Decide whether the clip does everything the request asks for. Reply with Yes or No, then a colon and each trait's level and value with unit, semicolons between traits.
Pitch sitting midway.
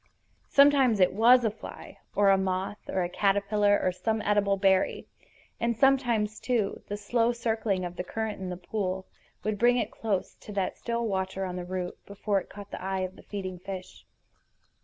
No: high, 200 Hz